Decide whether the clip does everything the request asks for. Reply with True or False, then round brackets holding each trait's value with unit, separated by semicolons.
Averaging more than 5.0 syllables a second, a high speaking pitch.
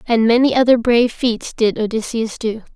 True (5.2 syllables/s; 230 Hz)